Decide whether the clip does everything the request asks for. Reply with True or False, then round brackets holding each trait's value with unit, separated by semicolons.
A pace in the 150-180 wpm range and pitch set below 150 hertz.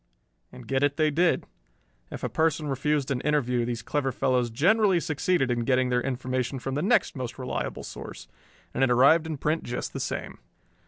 False (190 wpm; 135 Hz)